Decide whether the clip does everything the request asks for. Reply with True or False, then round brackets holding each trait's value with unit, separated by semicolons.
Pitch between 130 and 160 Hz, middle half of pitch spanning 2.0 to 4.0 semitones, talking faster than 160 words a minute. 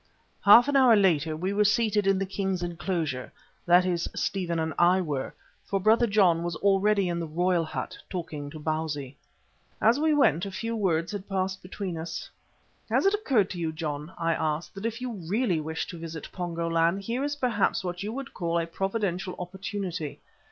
False (185 Hz; 3.7 semitones; 195 wpm)